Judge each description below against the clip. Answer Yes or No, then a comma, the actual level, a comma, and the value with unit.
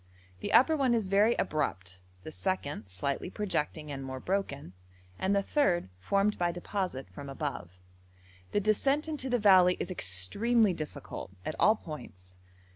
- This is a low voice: No, medium, 180 Hz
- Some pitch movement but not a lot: No, wide, 7.5 semitones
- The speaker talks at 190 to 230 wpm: No, average, 150 wpm